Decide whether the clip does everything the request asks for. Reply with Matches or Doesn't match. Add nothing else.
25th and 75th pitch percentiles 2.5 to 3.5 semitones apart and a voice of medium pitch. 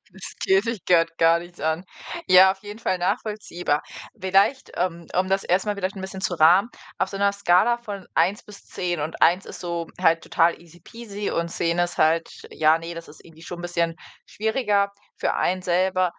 Matches